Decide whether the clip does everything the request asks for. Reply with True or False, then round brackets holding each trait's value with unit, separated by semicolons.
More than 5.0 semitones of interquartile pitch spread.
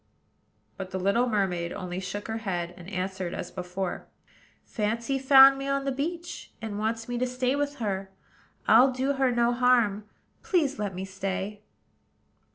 True (5.4 semitones)